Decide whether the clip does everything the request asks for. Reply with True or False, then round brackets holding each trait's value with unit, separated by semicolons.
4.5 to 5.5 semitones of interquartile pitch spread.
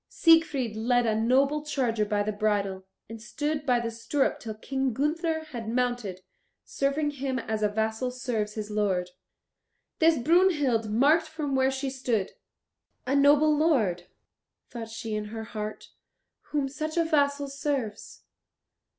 True (4.9 semitones)